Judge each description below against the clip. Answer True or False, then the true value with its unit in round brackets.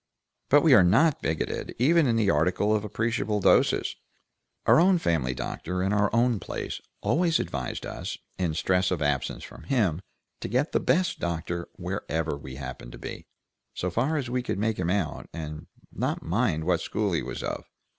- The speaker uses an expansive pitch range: True (6.9 semitones)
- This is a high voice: False (95 Hz)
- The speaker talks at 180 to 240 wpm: True (185 wpm)